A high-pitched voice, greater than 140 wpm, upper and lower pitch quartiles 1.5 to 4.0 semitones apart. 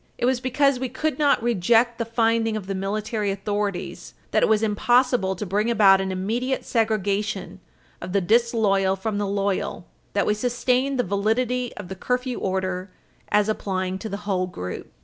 Yes: high, 210 Hz; average, 175 wpm; average, 3.6 semitones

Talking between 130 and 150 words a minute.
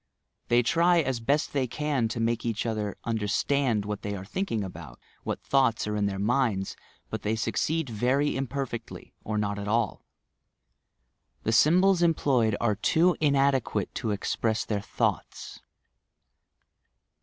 Yes: average, 145 wpm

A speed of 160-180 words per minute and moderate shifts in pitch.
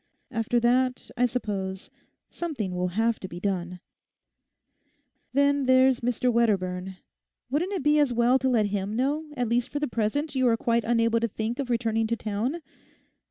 Yes: average, 175 wpm; average, 3.5 semitones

